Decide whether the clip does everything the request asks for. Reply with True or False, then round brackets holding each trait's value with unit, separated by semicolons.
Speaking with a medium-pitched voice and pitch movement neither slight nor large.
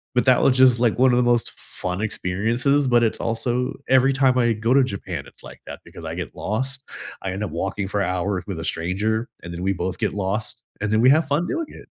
False (115 Hz; 4.8 semitones)